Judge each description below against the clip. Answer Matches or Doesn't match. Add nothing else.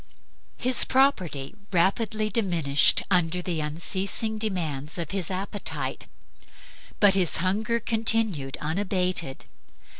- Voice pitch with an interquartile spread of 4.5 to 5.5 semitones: Matches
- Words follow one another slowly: Matches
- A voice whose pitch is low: Doesn't match